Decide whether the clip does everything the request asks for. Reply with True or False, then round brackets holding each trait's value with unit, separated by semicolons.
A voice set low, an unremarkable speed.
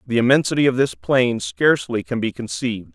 True (120 Hz; 185 wpm)